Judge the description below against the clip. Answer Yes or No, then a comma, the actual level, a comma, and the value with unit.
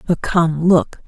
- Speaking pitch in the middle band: Yes, medium, 165 Hz